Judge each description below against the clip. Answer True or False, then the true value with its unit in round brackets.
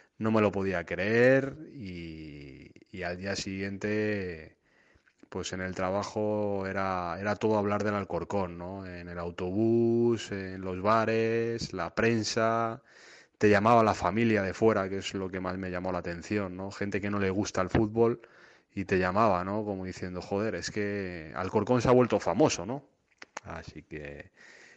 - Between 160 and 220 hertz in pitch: False (100 Hz)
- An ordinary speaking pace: True (165 wpm)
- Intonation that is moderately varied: True (3.0 semitones)